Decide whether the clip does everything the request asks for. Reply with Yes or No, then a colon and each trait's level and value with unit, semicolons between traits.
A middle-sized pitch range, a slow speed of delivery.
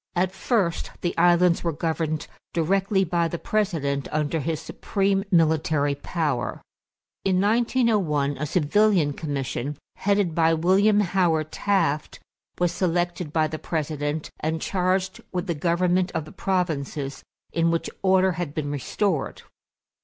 Yes: average, 3.5 semitones; slow, 130 wpm